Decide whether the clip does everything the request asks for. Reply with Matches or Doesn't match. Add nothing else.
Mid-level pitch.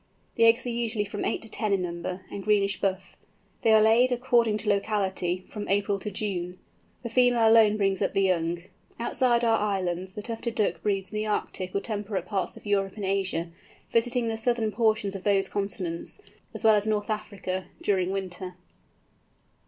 Doesn't match